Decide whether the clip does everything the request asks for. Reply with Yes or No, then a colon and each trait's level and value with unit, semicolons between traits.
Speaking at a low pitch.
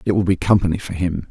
Yes: very low, 90 Hz